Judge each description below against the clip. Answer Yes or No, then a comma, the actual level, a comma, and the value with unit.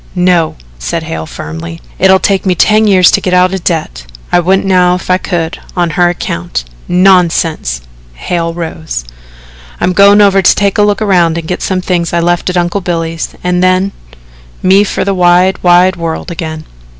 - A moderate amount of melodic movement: No, narrow, 2.1 semitones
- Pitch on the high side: No, medium, 180 Hz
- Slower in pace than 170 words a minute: No, average, 185 wpm